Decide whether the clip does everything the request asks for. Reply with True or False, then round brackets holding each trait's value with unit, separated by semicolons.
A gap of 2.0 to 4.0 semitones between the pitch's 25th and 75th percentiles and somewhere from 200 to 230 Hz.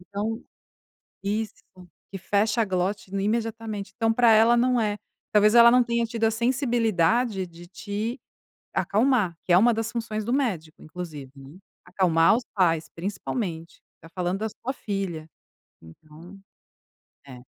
False (4.4 semitones; 210 Hz)